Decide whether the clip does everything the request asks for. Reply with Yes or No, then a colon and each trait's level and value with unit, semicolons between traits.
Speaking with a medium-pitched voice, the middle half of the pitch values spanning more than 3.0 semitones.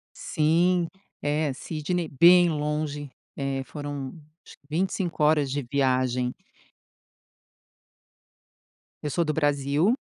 No: medium, 150 Hz; narrow, 2.6 semitones